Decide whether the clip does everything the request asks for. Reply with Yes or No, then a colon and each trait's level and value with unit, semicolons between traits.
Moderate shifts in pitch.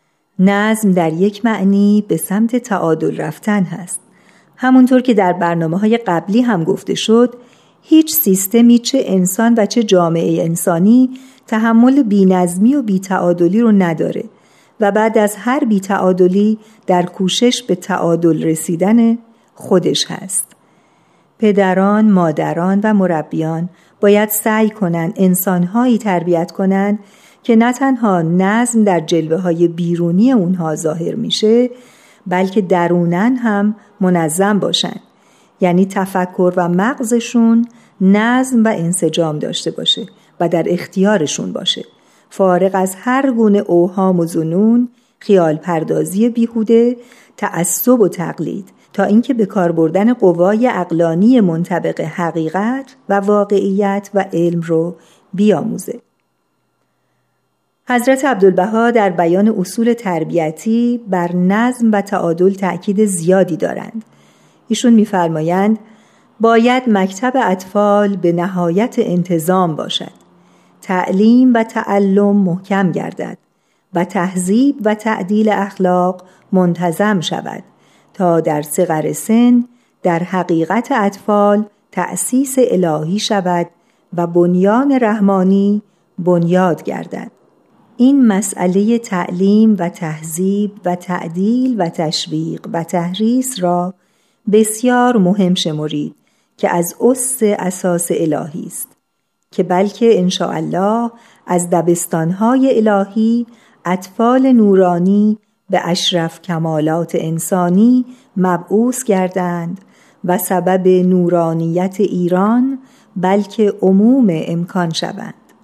Yes: average, 4.1 semitones